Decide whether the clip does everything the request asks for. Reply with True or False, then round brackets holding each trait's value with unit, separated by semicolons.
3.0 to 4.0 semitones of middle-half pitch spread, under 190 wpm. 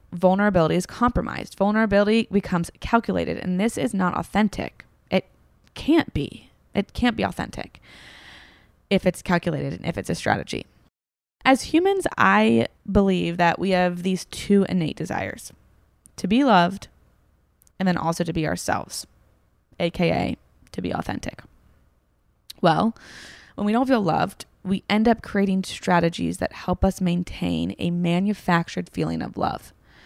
True (3.3 semitones; 140 wpm)